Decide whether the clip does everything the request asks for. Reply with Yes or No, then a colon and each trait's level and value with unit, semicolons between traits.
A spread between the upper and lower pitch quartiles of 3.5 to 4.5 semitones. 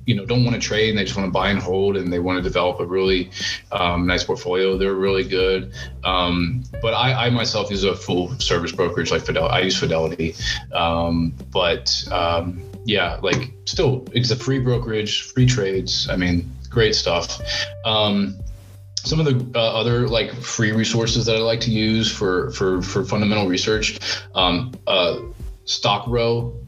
Yes: average, 3.8 semitones